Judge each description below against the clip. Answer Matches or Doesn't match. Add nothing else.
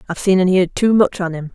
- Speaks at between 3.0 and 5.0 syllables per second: Doesn't match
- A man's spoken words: Doesn't match